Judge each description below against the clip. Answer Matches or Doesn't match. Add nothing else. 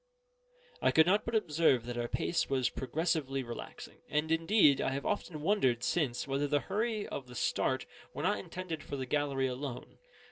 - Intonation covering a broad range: Doesn't match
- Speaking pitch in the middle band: Matches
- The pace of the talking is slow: Doesn't match